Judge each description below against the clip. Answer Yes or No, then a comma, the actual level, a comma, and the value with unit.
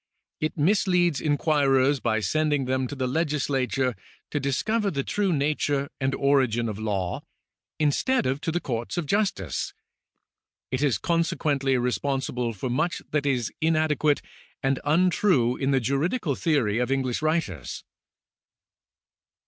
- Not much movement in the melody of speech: No, average, 3.5 semitones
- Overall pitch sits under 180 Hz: Yes, medium, 140 Hz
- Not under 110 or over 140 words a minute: Yes, slow, 135 wpm